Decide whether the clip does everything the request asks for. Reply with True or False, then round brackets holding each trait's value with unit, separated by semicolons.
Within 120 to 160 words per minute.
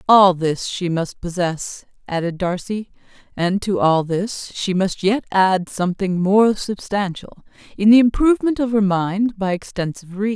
True (155 wpm)